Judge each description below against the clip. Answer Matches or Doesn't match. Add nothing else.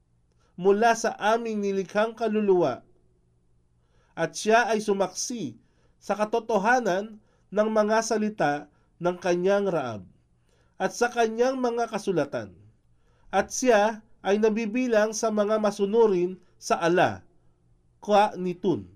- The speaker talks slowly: Matches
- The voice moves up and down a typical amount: Doesn't match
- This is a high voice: Matches